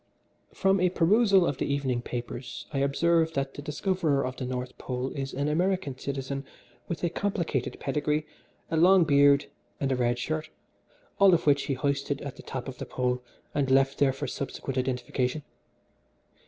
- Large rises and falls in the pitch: No, average, 3.6 semitones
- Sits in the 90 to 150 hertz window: Yes, medium, 140 Hz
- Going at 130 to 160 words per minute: No, average, 175 wpm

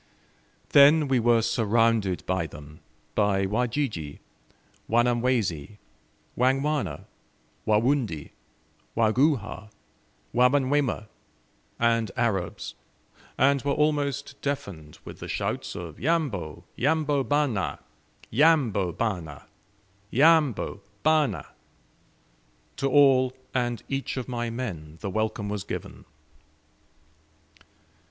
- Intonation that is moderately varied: No, wide, 5.8 semitones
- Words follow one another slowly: Yes, slow, 90 wpm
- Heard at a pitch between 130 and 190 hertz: No, low, 120 Hz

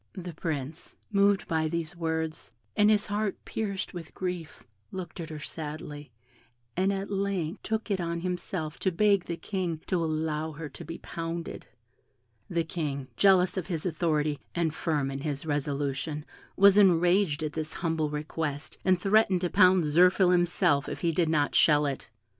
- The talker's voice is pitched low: No, medium, 165 Hz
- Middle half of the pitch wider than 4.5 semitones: No, average, 3.3 semitones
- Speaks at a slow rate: No, average, 165 wpm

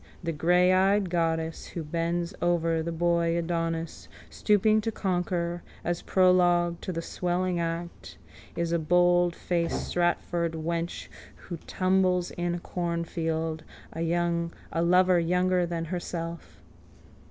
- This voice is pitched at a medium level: Yes, medium, 170 Hz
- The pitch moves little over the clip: Yes, narrow, 1.2 semitones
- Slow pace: Yes, slow, 115 wpm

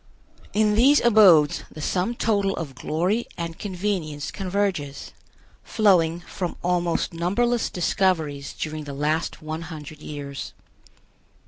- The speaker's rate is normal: No, slow, 115 wpm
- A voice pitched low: No, medium, 175 Hz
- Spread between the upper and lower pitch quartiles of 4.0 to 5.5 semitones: Yes, average, 4.7 semitones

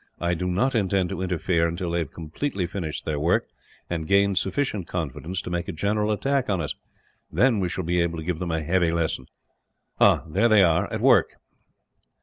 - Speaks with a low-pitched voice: Yes, very low, 90 Hz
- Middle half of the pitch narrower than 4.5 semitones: Yes, average, 3.1 semitones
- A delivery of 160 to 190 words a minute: No, average, 200 wpm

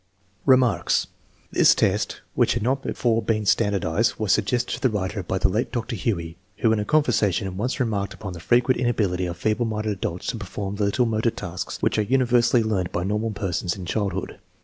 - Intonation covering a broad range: No, average, 3.7 semitones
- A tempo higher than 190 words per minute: Yes, average, 200 wpm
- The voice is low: Yes, low, 105 Hz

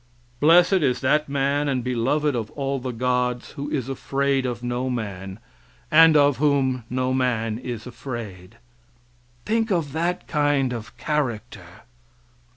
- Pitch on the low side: Yes, low, 130 Hz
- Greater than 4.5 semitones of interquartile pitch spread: No, average, 3.3 semitones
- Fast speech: No, average, 140 wpm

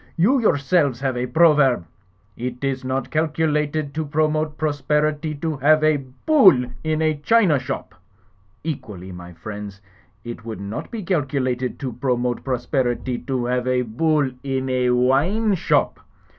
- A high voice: No, low, 135 Hz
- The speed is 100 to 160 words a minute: Yes, average, 150 wpm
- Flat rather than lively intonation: No, average, 3.7 semitones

